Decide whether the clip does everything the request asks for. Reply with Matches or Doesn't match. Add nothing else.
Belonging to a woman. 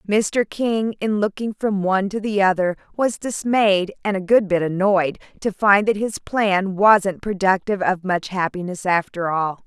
Matches